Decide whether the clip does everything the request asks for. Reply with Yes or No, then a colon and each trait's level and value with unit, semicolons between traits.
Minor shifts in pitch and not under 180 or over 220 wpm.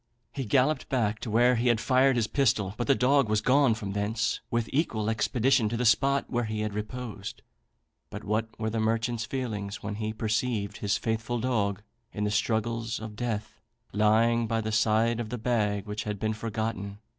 Yes: narrow, 2.2 semitones; average, 190 wpm